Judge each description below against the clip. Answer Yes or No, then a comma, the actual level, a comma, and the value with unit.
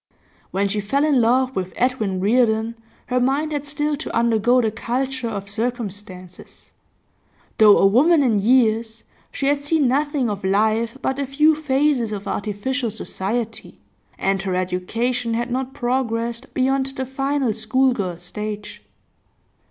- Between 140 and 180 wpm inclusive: Yes, average, 145 wpm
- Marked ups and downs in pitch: No, average, 4.0 semitones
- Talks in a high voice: Yes, high, 235 Hz